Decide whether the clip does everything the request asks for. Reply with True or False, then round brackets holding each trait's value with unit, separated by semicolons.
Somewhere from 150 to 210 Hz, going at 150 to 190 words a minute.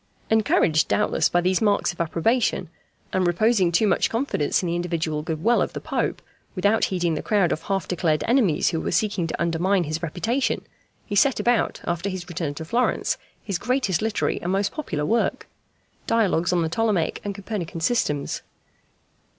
True (185 Hz; 175 wpm)